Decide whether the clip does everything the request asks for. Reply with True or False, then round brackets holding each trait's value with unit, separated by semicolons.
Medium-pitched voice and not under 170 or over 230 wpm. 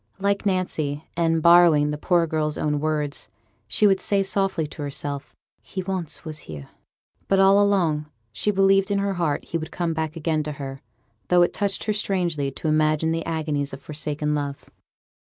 True (160 Hz; 180 wpm)